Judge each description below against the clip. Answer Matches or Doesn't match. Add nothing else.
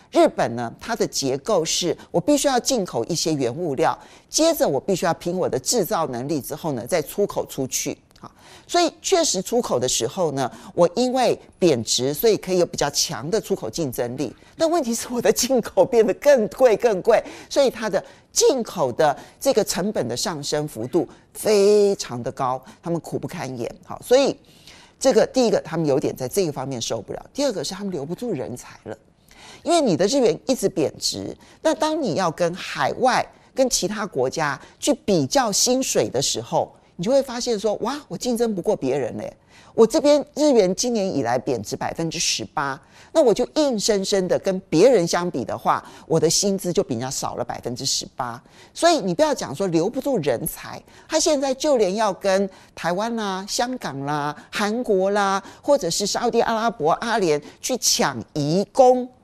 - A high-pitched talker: Matches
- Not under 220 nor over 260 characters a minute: Doesn't match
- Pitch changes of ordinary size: Doesn't match